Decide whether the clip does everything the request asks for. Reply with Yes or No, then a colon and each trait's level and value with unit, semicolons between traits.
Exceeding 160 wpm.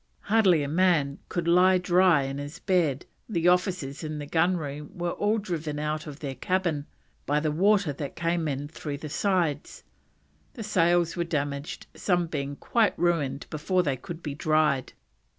Yes: average, 175 wpm